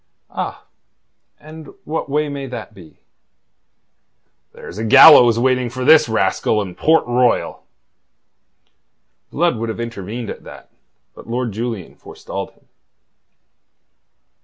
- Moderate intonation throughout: Yes, average, 4.1 semitones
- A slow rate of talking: Yes, slow, 115 wpm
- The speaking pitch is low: Yes, low, 120 Hz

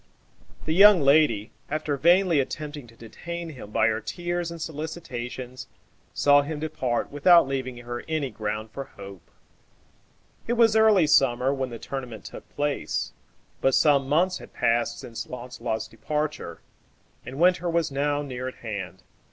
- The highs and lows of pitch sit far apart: No, average, 4.9 semitones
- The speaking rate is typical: Yes, average, 150 wpm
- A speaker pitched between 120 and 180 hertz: Yes, medium, 140 Hz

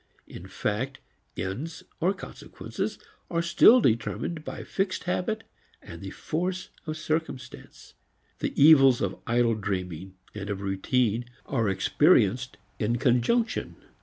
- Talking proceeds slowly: Yes, slow, 120 wpm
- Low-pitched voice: Yes, low, 125 Hz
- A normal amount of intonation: No, wide, 7.9 semitones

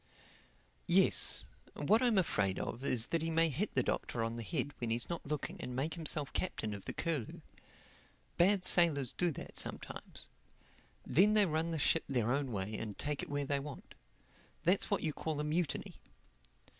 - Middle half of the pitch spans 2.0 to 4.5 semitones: No, average, 5.2 semitones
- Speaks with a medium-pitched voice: Yes, medium, 150 Hz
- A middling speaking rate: Yes, average, 180 wpm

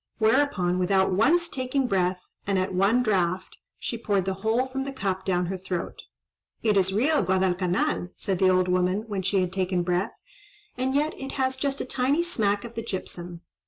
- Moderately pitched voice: No, high, 195 Hz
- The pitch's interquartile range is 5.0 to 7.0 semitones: Yes, wide, 5.4 semitones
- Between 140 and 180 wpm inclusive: No, average, 190 wpm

